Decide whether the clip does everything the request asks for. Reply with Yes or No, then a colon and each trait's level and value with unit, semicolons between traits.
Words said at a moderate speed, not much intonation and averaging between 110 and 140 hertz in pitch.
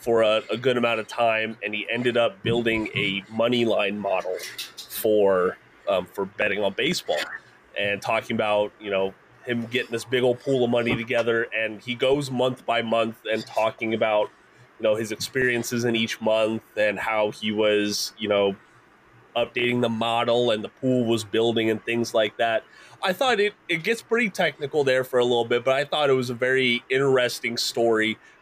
Yes: average, 190 wpm; narrow, 2.2 semitones; low, 115 Hz